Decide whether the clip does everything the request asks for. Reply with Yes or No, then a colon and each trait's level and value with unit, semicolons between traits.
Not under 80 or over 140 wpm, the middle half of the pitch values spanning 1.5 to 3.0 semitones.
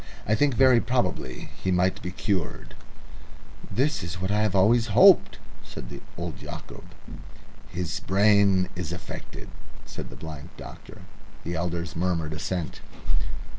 No: slow, 135 wpm; average, 3.9 semitones